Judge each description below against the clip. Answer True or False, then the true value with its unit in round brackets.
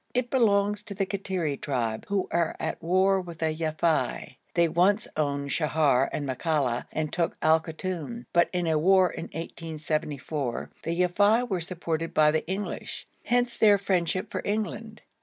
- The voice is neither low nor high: True (170 Hz)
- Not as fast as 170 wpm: True (160 wpm)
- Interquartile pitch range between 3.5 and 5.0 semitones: True (4.2 semitones)